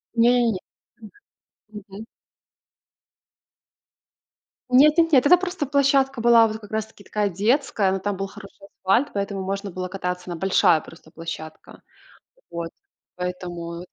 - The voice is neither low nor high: No, high, 200 Hz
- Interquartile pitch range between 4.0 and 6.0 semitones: Yes, average, 4.9 semitones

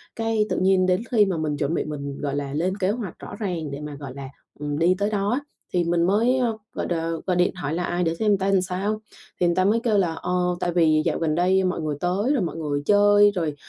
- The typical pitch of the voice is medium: Yes, medium, 180 Hz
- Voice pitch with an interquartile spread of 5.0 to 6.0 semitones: No, average, 4.6 semitones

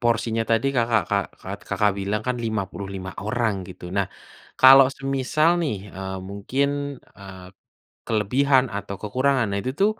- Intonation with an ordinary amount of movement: Yes, average, 4.8 semitones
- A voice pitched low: Yes, low, 110 Hz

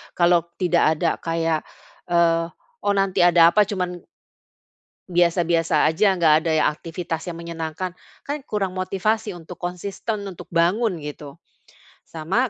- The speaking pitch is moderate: Yes, medium, 175 Hz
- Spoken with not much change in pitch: Yes, narrow, 2.2 semitones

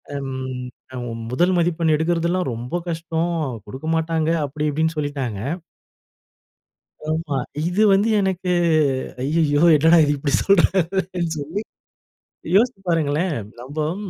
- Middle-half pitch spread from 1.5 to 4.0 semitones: Yes, average, 3.3 semitones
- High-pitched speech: No, medium, 160 Hz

